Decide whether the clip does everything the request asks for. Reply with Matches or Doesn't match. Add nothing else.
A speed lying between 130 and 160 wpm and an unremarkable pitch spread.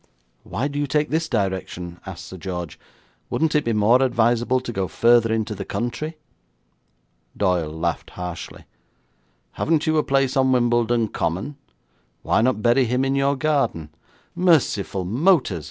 Doesn't match